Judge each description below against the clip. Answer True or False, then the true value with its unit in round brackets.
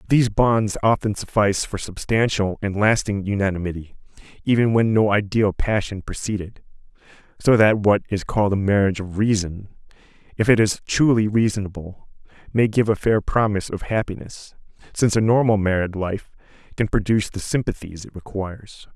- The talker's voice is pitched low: True (105 Hz)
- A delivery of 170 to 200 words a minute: False (150 wpm)